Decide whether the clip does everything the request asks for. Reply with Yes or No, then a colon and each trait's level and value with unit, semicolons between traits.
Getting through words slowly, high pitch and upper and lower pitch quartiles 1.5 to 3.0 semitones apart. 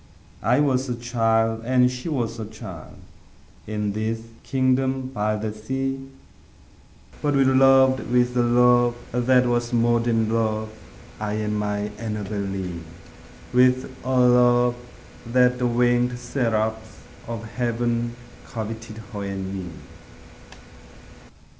No: slow, 120 wpm; low, 120 Hz; narrow, 2.5 semitones